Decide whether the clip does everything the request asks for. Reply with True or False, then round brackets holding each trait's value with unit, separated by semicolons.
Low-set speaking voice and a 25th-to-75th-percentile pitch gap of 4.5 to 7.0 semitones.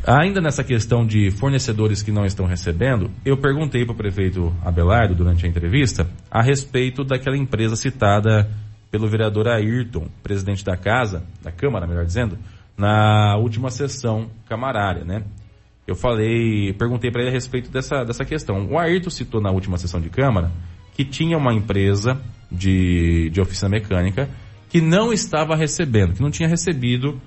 True (110 Hz; 5.0 semitones)